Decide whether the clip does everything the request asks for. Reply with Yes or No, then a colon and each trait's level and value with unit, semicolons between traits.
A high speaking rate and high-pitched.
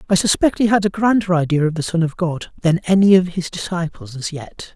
No: fast, 240 wpm; medium, 175 Hz